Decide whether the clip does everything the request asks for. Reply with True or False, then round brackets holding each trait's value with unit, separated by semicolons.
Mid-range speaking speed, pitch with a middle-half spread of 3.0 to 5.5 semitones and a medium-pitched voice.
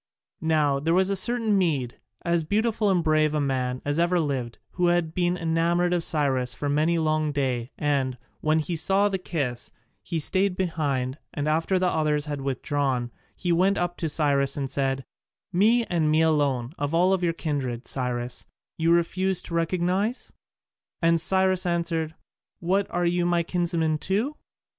True (170 wpm; 3.8 semitones; 165 Hz)